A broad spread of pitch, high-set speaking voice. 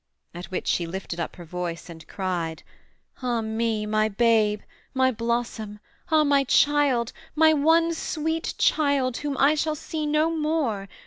Yes: wide, 6.6 semitones; high, 240 Hz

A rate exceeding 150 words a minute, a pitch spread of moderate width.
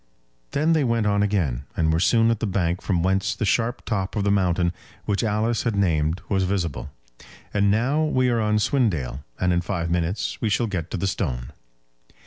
Yes: average, 200 wpm; average, 4.6 semitones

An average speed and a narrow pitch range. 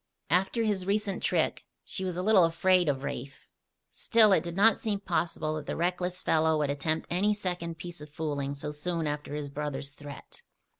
No: average, 190 wpm; average, 4.1 semitones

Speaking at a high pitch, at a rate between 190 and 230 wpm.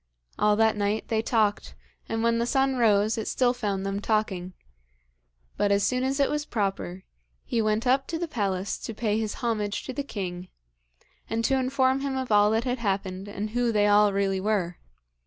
Yes: high, 215 Hz; average, 195 wpm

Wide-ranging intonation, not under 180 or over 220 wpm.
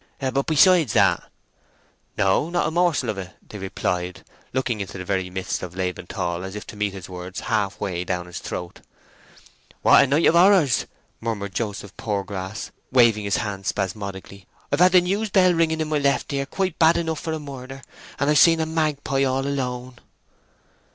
Yes: wide, 8.2 semitones; average, 185 wpm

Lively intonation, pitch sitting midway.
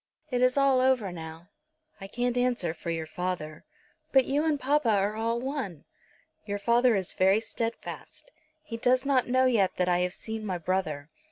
No: wide, 5.9 semitones; high, 225 Hz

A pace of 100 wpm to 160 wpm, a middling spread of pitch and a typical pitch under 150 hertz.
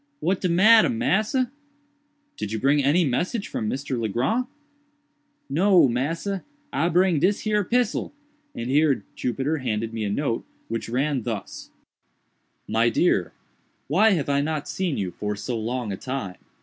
No: average, 150 wpm; wide, 8.2 semitones; medium, 140 Hz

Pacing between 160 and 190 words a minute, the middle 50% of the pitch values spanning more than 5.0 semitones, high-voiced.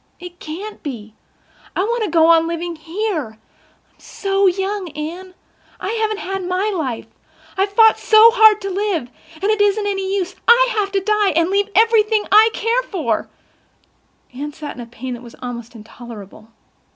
Yes: average, 165 wpm; wide, 5.5 semitones; very high, 380 Hz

